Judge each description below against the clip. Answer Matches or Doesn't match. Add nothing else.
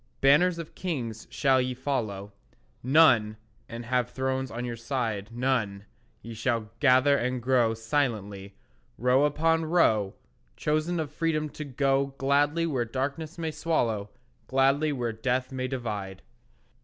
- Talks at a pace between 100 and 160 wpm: Matches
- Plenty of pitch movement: Doesn't match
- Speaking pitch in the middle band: Doesn't match